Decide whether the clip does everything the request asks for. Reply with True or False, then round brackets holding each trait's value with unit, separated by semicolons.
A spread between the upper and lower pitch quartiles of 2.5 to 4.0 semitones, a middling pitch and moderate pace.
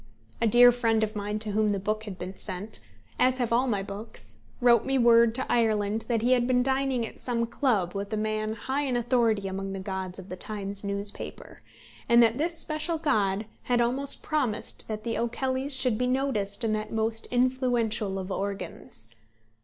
False (3.4 semitones; 225 Hz; 190 wpm)